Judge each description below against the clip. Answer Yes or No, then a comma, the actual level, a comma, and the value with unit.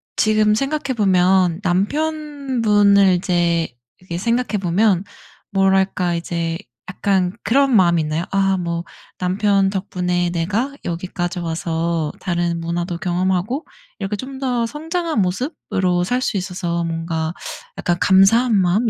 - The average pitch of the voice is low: No, high, 190 Hz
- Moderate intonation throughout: Yes, average, 3.8 semitones